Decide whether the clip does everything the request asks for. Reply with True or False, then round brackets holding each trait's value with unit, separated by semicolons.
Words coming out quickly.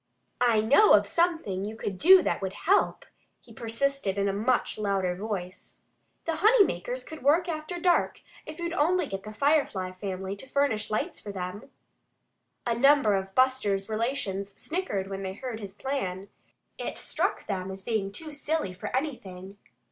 False (170 wpm)